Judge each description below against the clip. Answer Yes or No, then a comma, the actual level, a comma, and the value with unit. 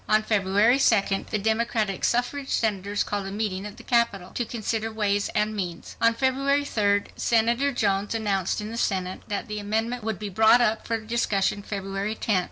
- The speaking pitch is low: No, high, 215 Hz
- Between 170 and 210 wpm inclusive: Yes, average, 180 wpm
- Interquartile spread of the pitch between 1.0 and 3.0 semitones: Yes, narrow, 2.5 semitones